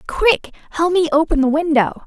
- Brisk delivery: No, average, 175 wpm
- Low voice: No, very high, 315 Hz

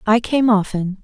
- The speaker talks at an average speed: Yes, average, 175 wpm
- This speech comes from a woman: Yes, female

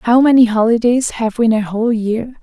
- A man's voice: No, female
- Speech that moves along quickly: Yes, fast, 225 wpm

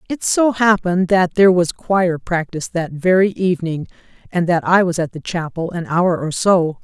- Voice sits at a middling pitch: Yes, medium, 175 Hz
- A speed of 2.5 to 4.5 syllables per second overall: No, 5.0 syllables/s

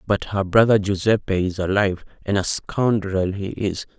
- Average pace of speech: Yes, average, 165 wpm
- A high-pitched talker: No, low, 100 Hz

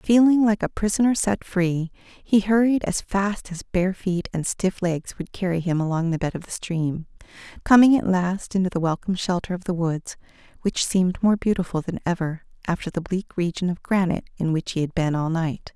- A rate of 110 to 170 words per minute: No, fast, 205 wpm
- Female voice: Yes, female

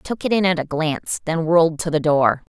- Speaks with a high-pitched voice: No, medium, 160 Hz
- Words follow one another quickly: Yes, fast, 285 wpm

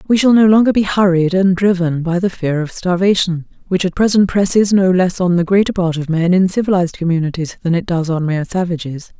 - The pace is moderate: No, fast, 220 wpm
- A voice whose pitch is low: No, medium, 180 Hz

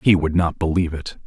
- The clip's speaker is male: Yes, male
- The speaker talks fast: Yes, fast, 240 wpm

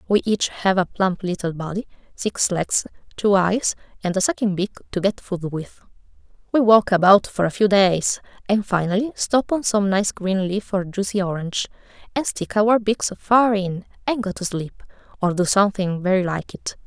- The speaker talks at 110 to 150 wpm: No, average, 190 wpm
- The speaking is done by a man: No, female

